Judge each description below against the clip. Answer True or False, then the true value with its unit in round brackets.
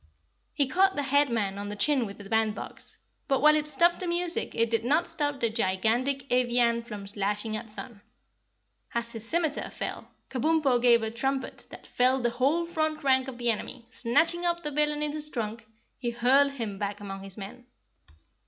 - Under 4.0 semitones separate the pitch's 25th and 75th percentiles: False (4.9 semitones)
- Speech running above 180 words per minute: True (190 wpm)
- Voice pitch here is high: True (250 Hz)